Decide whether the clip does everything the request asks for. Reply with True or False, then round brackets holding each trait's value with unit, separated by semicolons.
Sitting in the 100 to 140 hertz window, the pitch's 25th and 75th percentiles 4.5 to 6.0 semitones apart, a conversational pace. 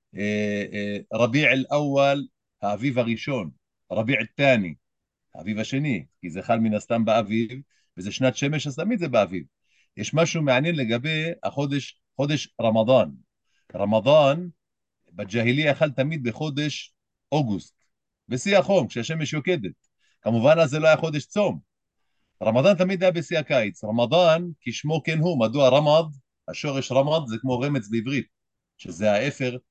True (135 Hz; 5.2 semitones; 130 wpm)